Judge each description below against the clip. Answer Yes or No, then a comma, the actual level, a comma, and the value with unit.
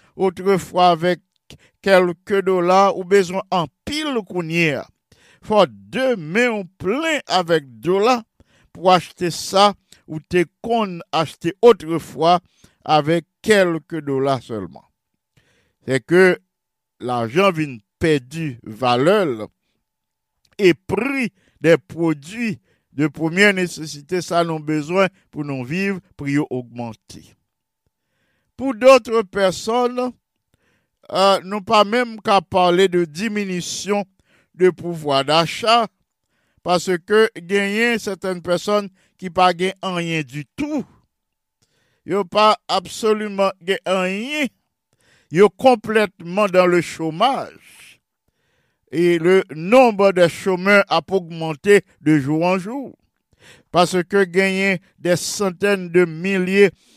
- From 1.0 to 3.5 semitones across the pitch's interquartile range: No, average, 3.9 semitones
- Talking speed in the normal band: No, slow, 105 wpm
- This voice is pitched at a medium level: Yes, medium, 180 Hz